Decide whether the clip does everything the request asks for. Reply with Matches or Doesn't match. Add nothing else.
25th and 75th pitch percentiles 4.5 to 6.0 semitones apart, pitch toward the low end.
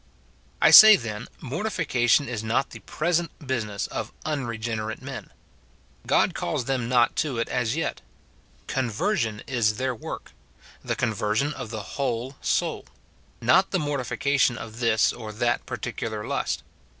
Doesn't match